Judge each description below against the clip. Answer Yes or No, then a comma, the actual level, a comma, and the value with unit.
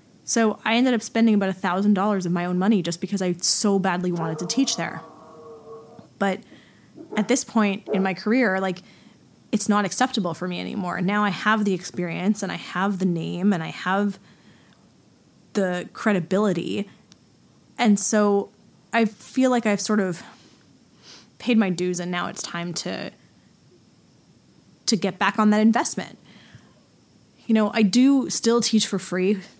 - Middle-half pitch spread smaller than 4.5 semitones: Yes, average, 3.2 semitones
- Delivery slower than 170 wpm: Yes, average, 160 wpm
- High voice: Yes, high, 200 Hz